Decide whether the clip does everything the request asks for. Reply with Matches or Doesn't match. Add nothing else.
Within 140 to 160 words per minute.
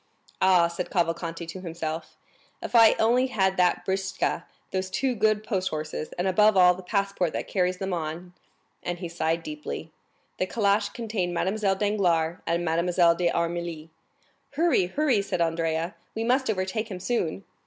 Matches